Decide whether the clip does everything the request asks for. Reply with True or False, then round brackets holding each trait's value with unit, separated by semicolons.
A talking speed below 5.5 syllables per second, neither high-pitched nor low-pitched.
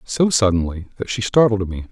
False (5.3 syllables/s; 105 Hz)